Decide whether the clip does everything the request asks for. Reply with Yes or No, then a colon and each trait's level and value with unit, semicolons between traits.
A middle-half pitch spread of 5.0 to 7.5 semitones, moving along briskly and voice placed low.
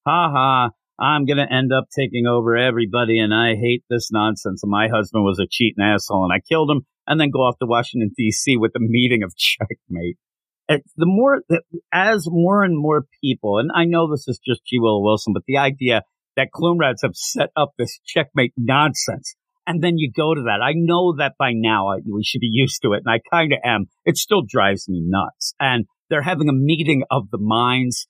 Yes: wide, 5.6 semitones; fast, 215 wpm; low, 125 Hz